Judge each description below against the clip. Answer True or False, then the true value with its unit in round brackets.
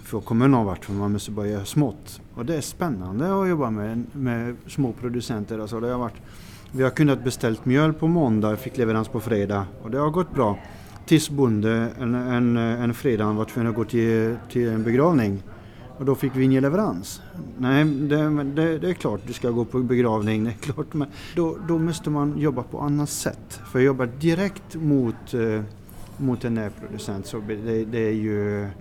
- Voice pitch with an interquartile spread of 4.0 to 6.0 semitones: True (4.3 semitones)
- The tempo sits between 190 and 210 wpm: True (195 wpm)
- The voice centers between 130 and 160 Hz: False (120 Hz)